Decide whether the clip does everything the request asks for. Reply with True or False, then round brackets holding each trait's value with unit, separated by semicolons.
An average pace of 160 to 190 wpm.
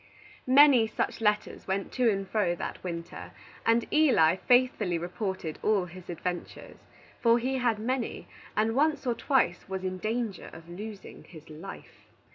False (150 wpm)